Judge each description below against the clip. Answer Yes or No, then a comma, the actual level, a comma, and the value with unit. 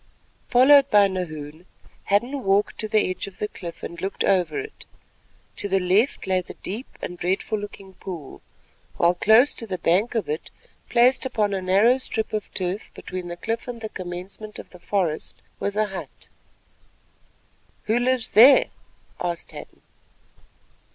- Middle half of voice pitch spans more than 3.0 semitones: Yes, average, 3.8 semitones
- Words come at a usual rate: Yes, average, 160 wpm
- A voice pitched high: Yes, high, 200 Hz